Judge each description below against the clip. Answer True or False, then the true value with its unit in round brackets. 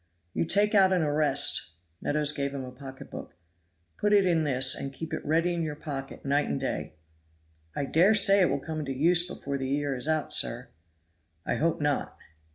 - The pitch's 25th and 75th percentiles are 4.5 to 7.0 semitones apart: False (3.6 semitones)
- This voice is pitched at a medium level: True (150 Hz)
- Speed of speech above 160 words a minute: True (195 wpm)